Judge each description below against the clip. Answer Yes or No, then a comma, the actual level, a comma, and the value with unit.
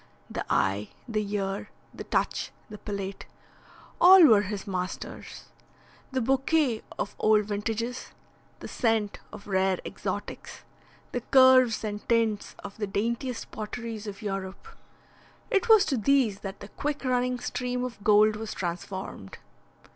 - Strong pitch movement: No, average, 3.8 semitones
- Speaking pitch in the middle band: No, high, 215 Hz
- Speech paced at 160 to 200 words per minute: No, slow, 135 wpm